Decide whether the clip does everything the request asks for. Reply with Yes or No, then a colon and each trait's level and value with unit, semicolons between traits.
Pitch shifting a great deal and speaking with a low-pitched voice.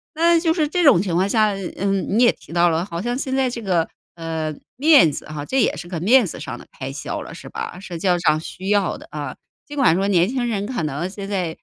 No: wide, 6.4 semitones; high, 195 Hz